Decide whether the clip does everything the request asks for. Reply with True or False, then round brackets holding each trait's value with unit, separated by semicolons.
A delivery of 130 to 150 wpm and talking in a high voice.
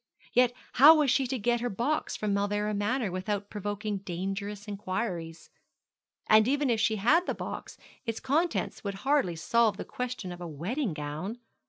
False (170 wpm; 210 Hz)